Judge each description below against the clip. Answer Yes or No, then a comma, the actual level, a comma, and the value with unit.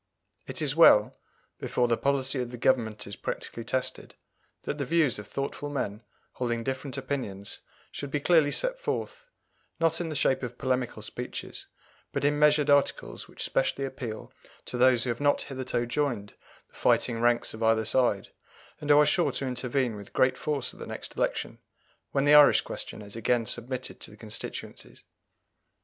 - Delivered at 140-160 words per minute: No, average, 175 wpm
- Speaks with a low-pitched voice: Yes, low, 130 Hz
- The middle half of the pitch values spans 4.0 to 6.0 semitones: No, average, 3.5 semitones